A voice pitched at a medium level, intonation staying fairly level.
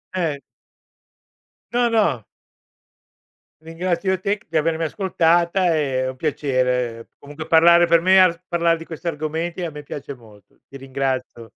No: medium, 160 Hz; average, 4.0 semitones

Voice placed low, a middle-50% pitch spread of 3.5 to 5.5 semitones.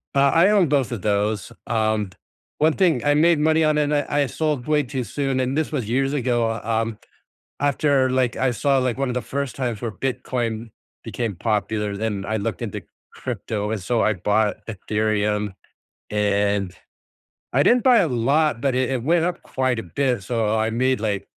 Yes: low, 120 Hz; average, 4.6 semitones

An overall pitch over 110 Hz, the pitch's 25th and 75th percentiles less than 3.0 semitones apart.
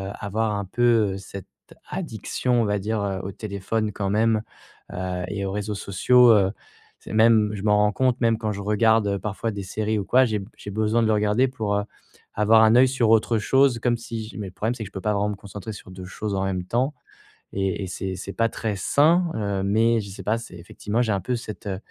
No: low, 105 Hz; narrow, 2.5 semitones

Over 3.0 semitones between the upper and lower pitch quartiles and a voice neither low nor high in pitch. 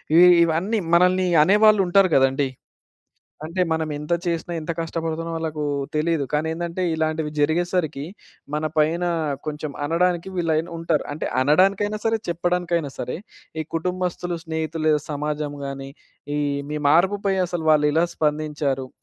No: average, 2.7 semitones; medium, 160 Hz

